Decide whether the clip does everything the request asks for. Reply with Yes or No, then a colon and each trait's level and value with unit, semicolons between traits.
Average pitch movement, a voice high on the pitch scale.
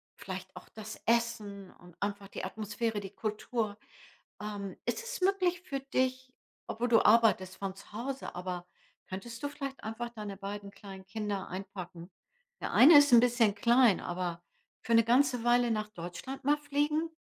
Yes: average, 4.3 semitones; high, 220 Hz